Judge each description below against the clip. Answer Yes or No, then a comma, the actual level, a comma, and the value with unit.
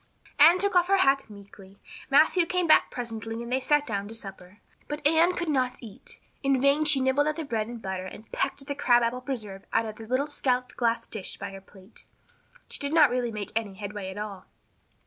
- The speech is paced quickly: Yes, fast, 225 wpm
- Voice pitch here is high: Yes, high, 245 Hz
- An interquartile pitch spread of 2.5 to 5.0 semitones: No, wide, 5.6 semitones